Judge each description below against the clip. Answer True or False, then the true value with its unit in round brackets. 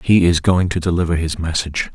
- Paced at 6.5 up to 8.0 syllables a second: False (5.8 syllables/s)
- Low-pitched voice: True (85 Hz)